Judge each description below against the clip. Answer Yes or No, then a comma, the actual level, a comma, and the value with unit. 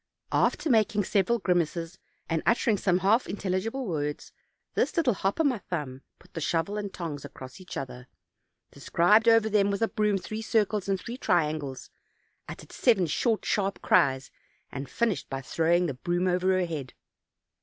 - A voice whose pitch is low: No, medium, 185 Hz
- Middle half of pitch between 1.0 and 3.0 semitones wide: No, average, 4.9 semitones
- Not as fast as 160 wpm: No, average, 165 wpm